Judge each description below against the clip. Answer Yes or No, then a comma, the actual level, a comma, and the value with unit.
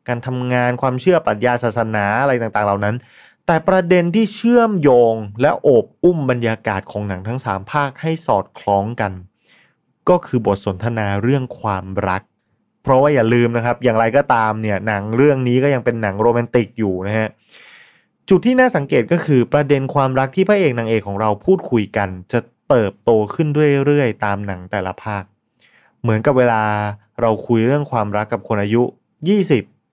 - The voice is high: No, low, 120 Hz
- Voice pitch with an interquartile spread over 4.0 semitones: Yes, average, 5.2 semitones